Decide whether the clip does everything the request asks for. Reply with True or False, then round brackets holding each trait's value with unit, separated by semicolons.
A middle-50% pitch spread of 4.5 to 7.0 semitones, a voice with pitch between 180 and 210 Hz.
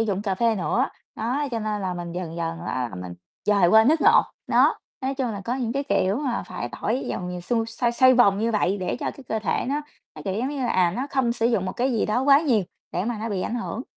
False (5.0 semitones; 225 Hz)